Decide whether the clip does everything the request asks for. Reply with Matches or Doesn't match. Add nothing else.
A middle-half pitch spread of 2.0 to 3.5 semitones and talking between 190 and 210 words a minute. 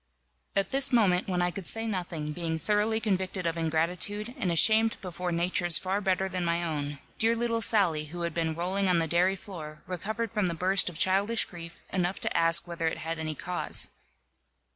Matches